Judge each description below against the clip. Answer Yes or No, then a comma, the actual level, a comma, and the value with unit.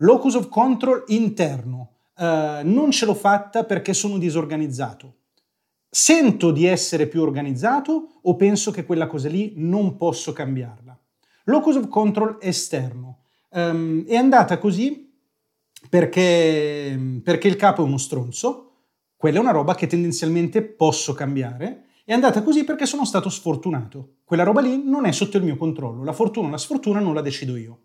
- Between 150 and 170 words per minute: Yes, average, 160 wpm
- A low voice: No, medium, 175 Hz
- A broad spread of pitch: Yes, wide, 6.5 semitones